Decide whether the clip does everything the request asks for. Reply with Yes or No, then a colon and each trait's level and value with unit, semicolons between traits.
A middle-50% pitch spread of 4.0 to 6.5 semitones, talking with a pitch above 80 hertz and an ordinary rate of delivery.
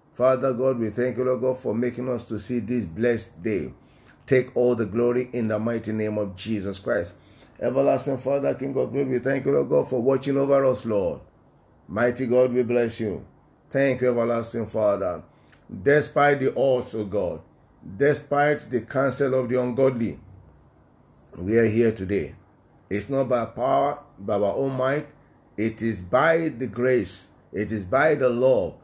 No: average, 2.9 semitones; low, 125 Hz; average, 170 wpm